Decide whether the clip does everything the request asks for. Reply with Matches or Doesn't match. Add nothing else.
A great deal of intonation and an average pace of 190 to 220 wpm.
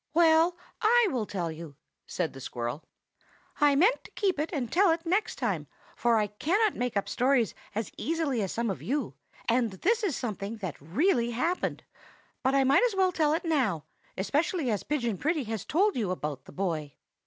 Matches